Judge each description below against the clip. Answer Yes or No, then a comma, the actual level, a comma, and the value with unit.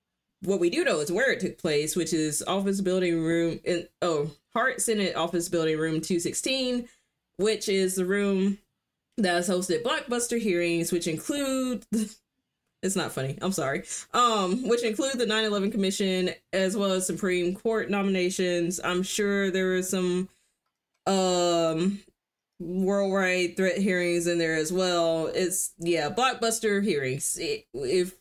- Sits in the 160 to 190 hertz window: Yes, medium, 185 Hz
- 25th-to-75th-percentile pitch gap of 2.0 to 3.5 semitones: Yes, average, 3.2 semitones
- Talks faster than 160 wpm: No, average, 150 wpm